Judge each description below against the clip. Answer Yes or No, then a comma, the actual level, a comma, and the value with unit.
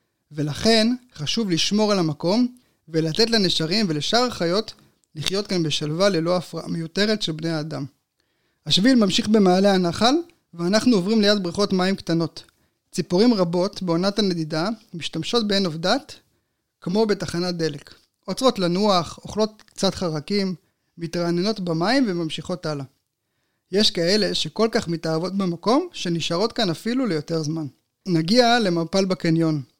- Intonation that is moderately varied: Yes, average, 4.6 semitones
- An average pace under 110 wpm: No, average, 125 wpm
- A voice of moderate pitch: Yes, medium, 180 Hz